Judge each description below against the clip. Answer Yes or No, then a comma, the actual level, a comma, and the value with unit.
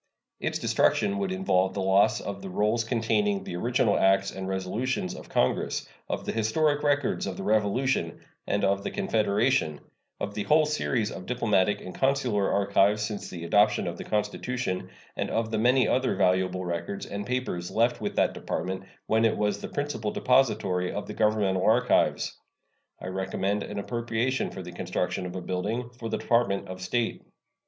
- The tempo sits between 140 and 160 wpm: No, average, 175 wpm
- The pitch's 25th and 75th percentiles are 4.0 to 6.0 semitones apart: Yes, average, 4.5 semitones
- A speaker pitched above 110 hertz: No, low, 105 Hz